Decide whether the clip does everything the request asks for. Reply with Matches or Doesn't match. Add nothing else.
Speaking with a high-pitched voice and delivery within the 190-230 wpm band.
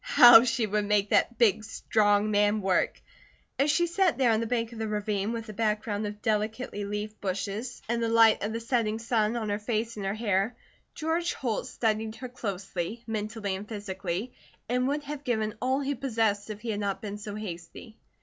Matches